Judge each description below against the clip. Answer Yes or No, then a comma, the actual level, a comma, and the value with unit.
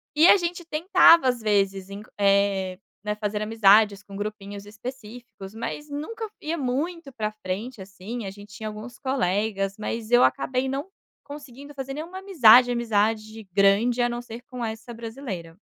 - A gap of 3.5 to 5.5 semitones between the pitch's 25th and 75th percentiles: Yes, average, 4.7 semitones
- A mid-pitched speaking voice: No, high, 225 Hz